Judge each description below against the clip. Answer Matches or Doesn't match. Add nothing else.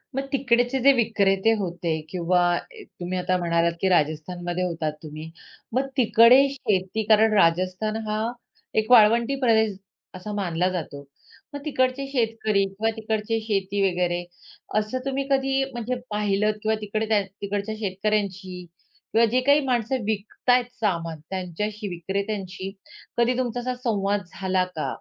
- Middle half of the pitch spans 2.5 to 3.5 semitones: Doesn't match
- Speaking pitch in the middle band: Doesn't match